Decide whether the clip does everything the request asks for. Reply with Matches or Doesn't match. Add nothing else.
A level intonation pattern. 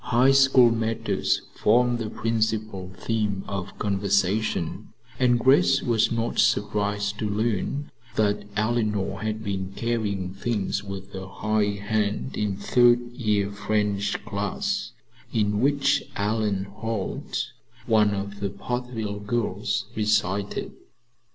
Matches